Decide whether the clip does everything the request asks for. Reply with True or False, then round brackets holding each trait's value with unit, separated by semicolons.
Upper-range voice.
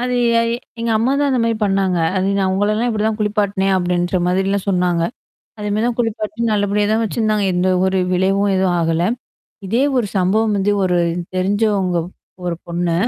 True (200 Hz)